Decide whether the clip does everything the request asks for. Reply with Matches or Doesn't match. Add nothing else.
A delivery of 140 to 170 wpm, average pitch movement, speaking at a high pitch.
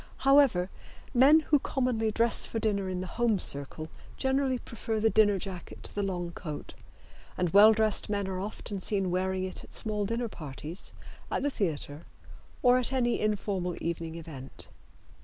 Matches